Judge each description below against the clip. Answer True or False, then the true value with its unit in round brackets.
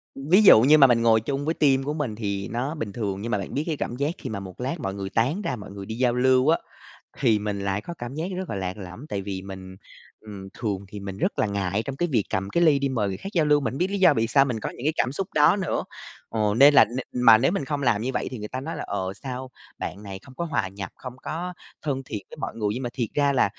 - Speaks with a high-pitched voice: False (120 Hz)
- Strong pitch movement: True (5.8 semitones)